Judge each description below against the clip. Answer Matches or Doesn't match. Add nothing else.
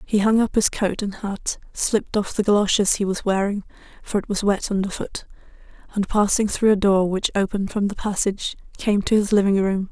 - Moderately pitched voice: Doesn't match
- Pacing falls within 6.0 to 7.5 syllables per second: Doesn't match